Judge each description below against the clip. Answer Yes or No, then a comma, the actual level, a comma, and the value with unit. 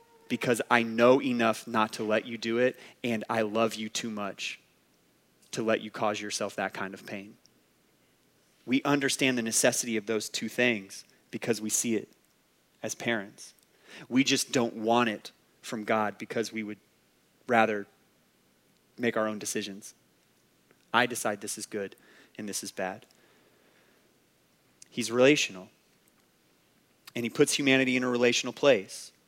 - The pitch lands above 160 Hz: No, low, 115 Hz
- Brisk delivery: No, average, 150 wpm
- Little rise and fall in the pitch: Yes, narrow, 2.3 semitones